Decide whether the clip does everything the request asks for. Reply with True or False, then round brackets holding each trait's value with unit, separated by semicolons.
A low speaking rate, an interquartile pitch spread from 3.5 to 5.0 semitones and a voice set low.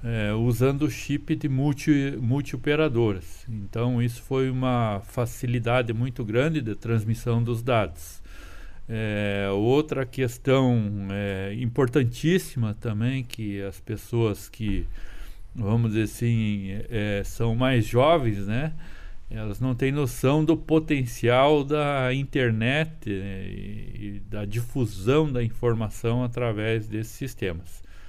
True (115 wpm; 4.2 semitones; 115 Hz)